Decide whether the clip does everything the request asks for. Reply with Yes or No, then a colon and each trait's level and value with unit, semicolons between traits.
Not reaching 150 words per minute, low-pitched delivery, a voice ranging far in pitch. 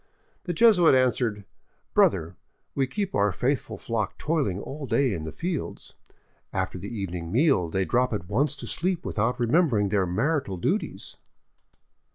No: average, 155 wpm; low, 115 Hz; wide, 7.2 semitones